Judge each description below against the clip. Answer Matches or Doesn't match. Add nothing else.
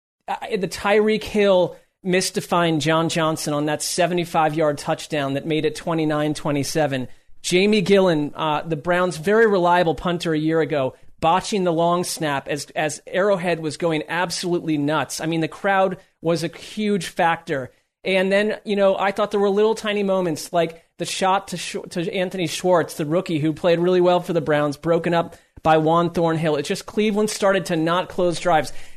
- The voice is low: Doesn't match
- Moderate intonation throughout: Matches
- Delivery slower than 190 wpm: Matches